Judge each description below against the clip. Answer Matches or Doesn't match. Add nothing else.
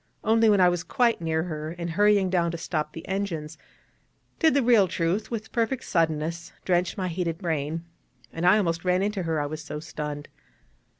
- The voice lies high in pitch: Doesn't match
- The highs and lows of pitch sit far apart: Doesn't match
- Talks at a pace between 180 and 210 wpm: Matches